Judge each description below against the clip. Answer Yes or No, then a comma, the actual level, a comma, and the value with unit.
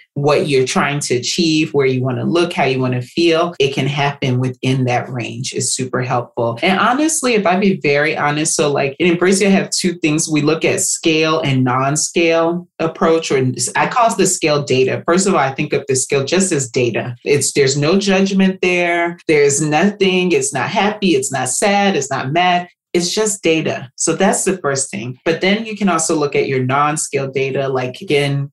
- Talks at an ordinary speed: No, fast, 210 wpm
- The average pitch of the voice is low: No, medium, 155 Hz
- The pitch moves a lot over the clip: No, average, 5.0 semitones